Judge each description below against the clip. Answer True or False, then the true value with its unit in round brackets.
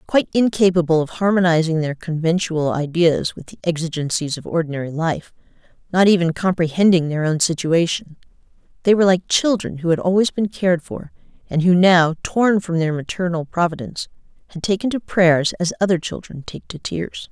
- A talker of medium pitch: True (175 Hz)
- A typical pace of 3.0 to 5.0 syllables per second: False (5.5 syllables/s)